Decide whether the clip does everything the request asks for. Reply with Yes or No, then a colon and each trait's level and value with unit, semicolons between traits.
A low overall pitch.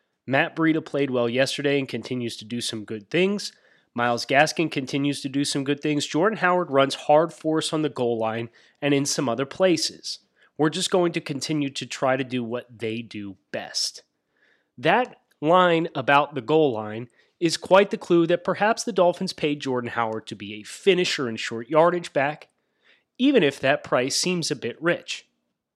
No: medium, 145 Hz